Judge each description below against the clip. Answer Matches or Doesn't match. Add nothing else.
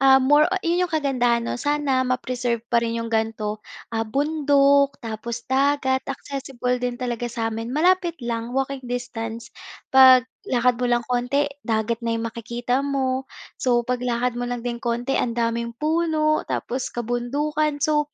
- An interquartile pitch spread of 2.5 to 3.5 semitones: Matches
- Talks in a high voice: Matches